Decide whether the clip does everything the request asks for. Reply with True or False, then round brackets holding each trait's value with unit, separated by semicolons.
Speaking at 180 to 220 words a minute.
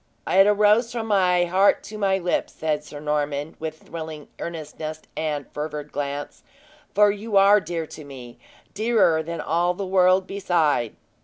False (155 wpm)